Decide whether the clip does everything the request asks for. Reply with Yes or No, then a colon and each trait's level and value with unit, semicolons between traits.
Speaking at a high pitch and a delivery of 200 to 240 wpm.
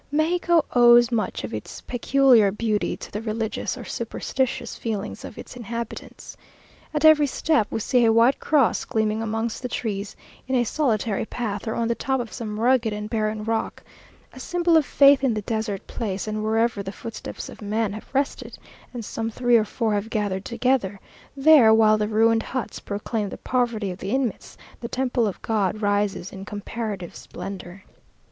No: high, 225 Hz; average, 180 wpm